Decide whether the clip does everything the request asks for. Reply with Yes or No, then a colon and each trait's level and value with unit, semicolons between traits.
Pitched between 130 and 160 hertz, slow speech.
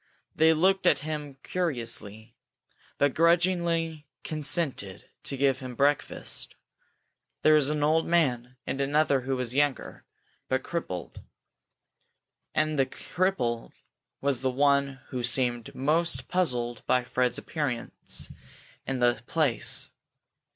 Yes: medium, 140 Hz; slow, 115 wpm